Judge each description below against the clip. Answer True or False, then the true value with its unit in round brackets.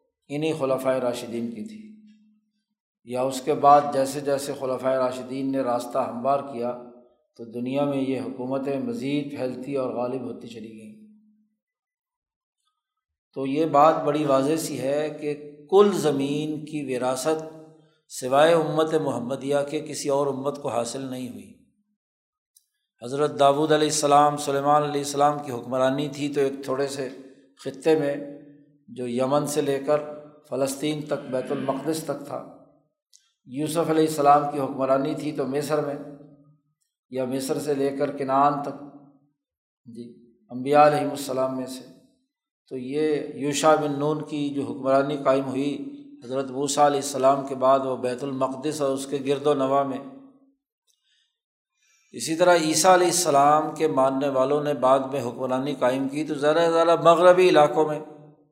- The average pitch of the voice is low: False (145 Hz)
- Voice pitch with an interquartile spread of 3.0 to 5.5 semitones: False (2.5 semitones)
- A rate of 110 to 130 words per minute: False (150 wpm)